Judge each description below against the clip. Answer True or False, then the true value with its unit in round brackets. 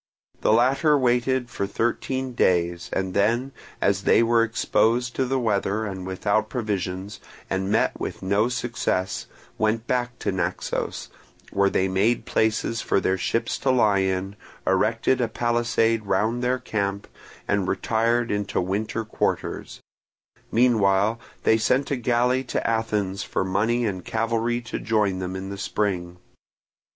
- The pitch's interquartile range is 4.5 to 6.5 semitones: False (3.5 semitones)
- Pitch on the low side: True (110 Hz)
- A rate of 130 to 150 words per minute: True (145 wpm)